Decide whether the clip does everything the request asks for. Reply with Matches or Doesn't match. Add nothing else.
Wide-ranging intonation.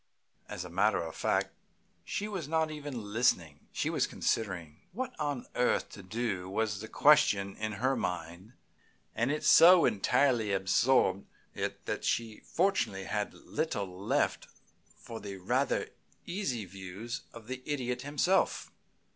Matches